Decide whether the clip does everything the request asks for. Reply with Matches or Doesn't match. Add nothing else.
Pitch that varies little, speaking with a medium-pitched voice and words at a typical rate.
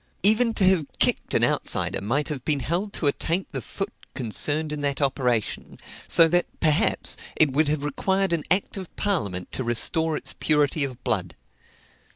Doesn't match